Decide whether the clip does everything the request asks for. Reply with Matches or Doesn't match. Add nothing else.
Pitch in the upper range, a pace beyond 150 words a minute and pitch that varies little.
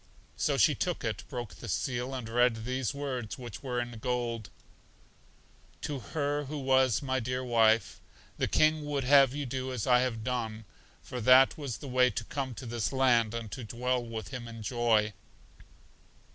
Doesn't match